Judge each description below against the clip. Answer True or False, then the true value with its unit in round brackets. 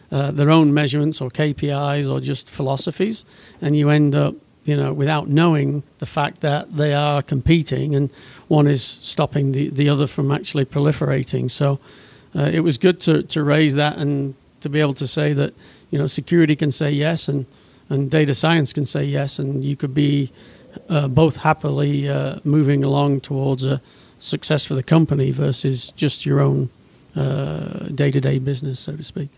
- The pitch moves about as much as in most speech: False (1.6 semitones)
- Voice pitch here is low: False (145 Hz)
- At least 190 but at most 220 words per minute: False (180 wpm)